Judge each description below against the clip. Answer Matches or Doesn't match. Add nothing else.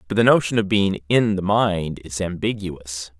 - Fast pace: Doesn't match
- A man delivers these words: Matches